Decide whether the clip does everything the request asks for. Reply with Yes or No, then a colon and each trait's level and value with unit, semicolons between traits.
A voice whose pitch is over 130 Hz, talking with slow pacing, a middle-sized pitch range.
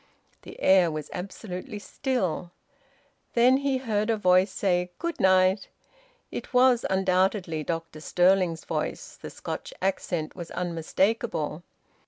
Yes: medium, 185 Hz; slow, 120 wpm; average, 3.5 semitones